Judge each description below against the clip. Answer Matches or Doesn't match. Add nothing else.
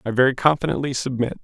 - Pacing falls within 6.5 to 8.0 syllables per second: Matches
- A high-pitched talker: Doesn't match